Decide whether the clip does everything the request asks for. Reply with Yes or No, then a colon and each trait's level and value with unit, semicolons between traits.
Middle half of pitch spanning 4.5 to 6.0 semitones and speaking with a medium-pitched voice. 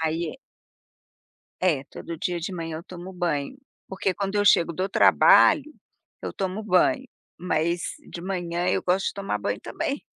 No: narrow, 2.6 semitones; medium, 180 Hz